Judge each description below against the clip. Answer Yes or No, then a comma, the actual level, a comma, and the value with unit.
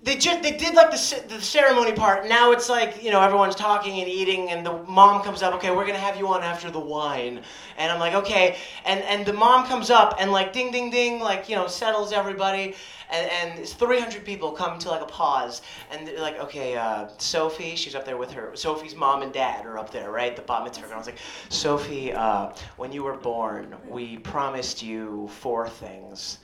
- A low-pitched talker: No, medium, 185 Hz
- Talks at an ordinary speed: No, fast, 225 wpm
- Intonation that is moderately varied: No, wide, 7.3 semitones